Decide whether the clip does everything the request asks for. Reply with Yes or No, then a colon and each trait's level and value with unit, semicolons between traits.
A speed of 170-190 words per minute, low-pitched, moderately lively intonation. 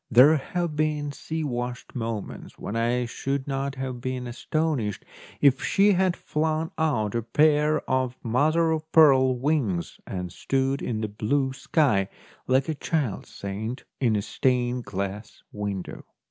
No: average, 145 wpm; low, 130 Hz; average, 4.8 semitones